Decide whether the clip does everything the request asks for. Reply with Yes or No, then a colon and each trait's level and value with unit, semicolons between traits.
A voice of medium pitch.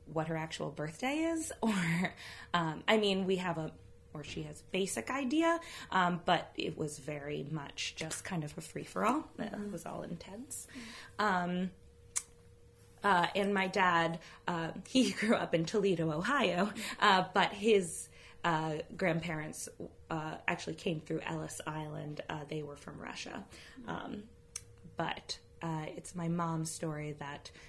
Yes: medium, 170 Hz